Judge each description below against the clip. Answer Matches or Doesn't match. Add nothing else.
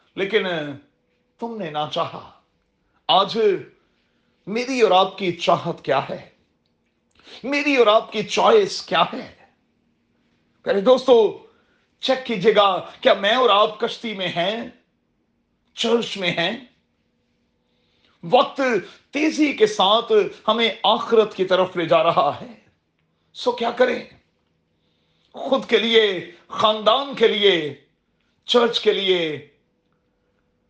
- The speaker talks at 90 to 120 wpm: Matches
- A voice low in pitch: Doesn't match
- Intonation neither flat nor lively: Doesn't match